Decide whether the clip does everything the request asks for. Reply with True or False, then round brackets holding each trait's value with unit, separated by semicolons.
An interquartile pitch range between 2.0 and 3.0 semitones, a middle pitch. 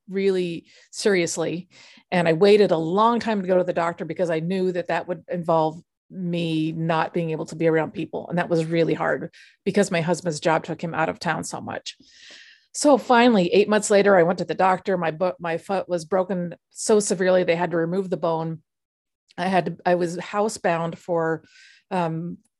True (2.4 semitones; 175 Hz)